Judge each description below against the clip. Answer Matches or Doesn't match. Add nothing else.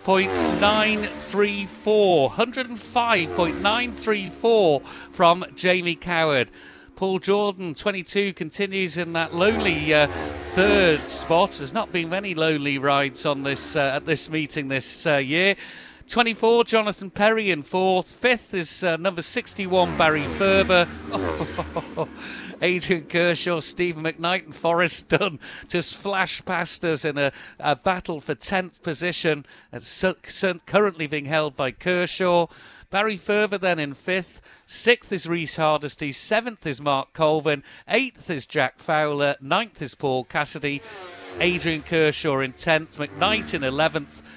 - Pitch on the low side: Doesn't match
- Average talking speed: Doesn't match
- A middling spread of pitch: Matches